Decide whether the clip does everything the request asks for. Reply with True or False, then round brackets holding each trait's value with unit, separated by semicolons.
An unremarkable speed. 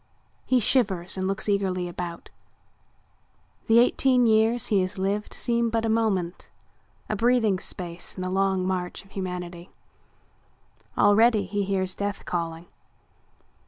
False (130 wpm)